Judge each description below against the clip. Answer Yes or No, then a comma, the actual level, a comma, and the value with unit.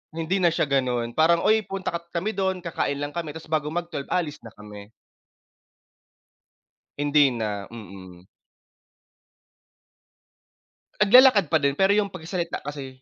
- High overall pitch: No, medium, 155 Hz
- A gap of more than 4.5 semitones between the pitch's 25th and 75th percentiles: Yes, average, 5.3 semitones